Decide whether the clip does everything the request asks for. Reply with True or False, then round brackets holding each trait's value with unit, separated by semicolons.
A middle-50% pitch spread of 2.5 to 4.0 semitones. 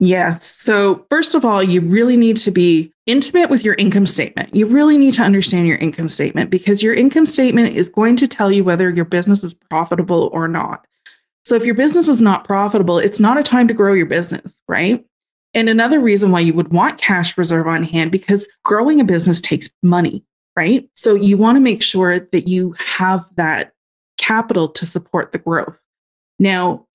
False (4.7 semitones)